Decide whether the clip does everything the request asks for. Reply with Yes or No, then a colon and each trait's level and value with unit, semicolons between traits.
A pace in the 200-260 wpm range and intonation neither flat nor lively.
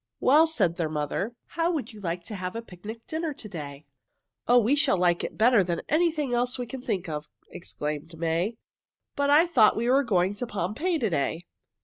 No: fast, 205 wpm; wide, 7.5 semitones